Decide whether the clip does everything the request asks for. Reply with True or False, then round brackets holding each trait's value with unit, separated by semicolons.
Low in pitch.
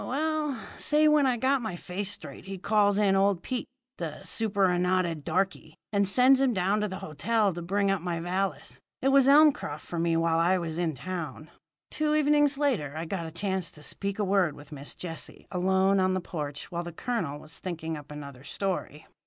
False (185 Hz)